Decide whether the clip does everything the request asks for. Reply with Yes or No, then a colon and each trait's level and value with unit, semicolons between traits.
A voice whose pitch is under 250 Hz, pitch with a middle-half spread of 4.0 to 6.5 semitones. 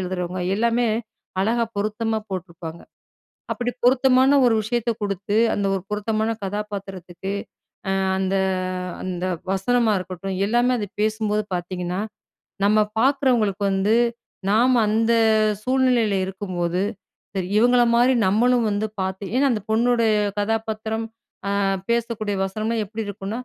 No: high, 215 Hz; average, 3.4 semitones